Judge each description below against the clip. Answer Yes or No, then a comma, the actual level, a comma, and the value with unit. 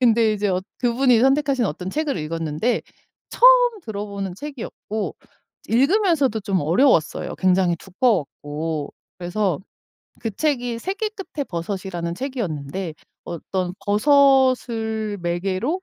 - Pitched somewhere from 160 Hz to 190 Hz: No, high, 215 Hz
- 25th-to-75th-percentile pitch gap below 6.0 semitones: No, wide, 6.9 semitones